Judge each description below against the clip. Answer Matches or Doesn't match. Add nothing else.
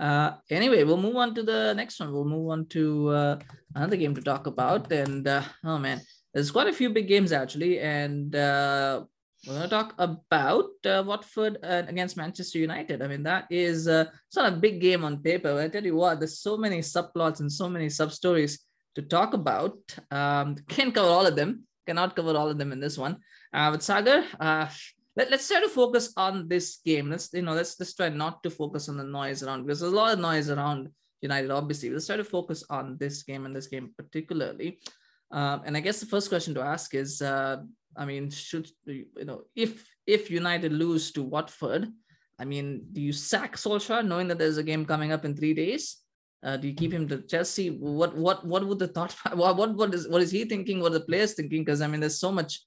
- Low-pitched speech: Doesn't match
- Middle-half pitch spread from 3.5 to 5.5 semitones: Matches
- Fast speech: Matches